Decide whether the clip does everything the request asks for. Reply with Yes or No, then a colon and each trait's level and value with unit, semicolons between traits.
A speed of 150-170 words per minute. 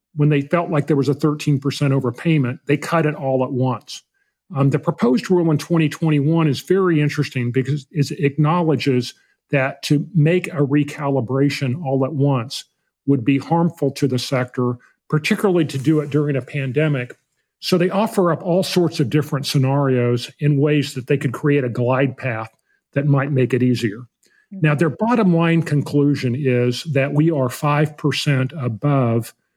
Yes: average, 165 wpm